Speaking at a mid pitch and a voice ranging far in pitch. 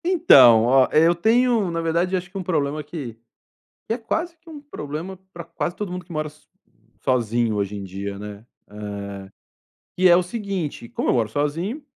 Yes: medium, 160 Hz; wide, 8.4 semitones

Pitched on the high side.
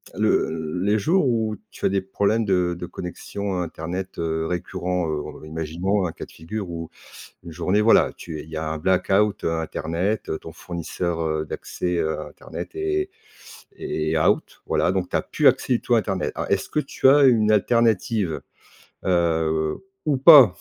No: very low, 90 Hz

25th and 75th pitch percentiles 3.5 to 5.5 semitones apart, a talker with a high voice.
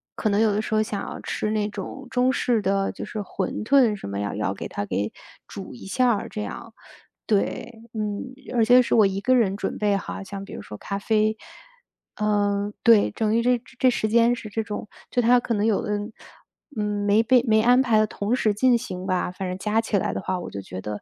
No: average, 2.7 semitones; high, 215 Hz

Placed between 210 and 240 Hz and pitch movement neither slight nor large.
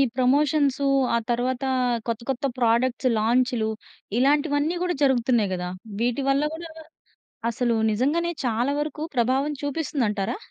No: very high, 260 Hz; average, 3.5 semitones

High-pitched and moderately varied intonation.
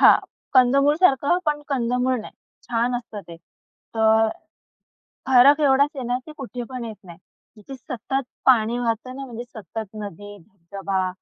Yes: high, 245 Hz; average, 3.6 semitones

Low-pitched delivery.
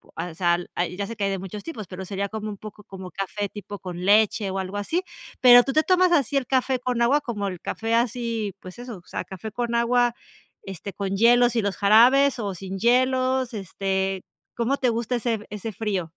No: high, 215 Hz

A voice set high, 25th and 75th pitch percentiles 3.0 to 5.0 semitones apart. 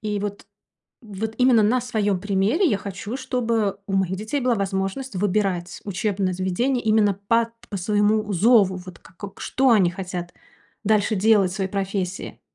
No: high, 205 Hz; narrow, 2.6 semitones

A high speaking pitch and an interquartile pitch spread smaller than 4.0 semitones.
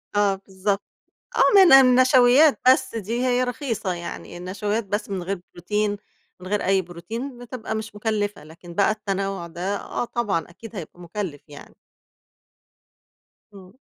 No: high, 205 Hz; average, 4.3 semitones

